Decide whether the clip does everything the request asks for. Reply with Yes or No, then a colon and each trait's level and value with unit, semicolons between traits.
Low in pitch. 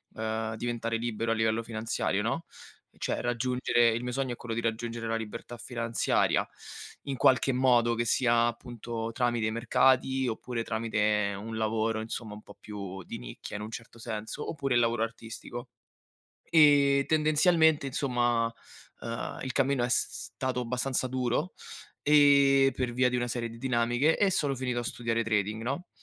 Yes: low, 120 Hz